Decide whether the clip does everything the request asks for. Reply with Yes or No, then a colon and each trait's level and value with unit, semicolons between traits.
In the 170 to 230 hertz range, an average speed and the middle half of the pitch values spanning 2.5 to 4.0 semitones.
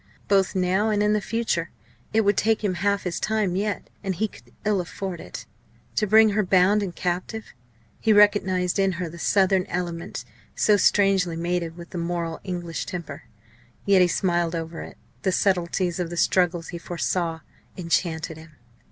Yes: medium, 185 Hz; average, 175 wpm; average, 2.8 semitones